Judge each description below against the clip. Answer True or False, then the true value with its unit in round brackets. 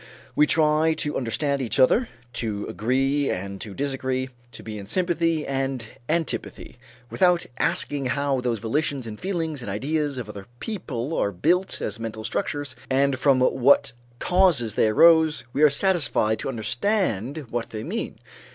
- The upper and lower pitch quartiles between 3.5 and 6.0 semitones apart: True (5.4 semitones)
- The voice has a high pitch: False (135 Hz)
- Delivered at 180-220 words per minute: False (155 wpm)